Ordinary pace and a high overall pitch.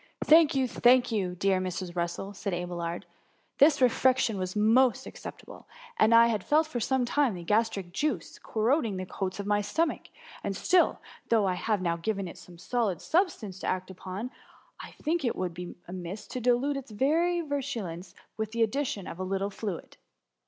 Yes: average, 190 wpm; high, 215 Hz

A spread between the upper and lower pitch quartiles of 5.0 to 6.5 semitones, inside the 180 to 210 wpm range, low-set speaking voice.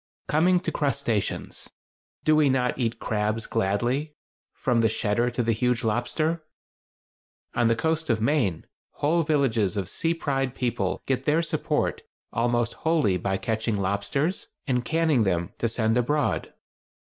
No: average, 5.3 semitones; average, 140 wpm; low, 120 Hz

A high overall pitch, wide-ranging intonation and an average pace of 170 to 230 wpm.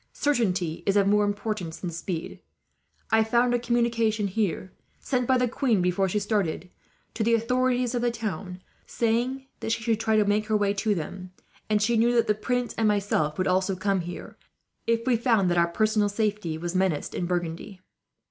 No: high, 210 Hz; average, 3.9 semitones; average, 185 wpm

